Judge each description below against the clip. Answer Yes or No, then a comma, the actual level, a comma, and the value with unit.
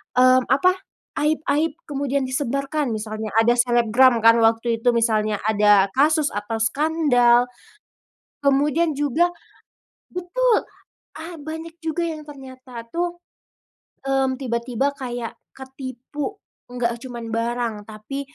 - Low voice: No, very high, 260 Hz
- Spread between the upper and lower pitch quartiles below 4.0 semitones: No, average, 4.3 semitones